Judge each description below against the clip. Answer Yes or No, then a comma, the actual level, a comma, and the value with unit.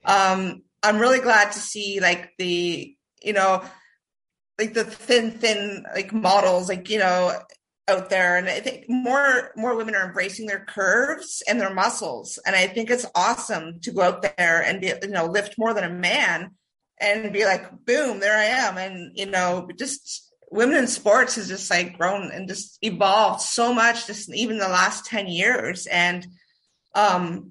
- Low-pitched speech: No, high, 200 Hz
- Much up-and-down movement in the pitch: No, average, 3.6 semitones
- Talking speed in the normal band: Yes, average, 180 wpm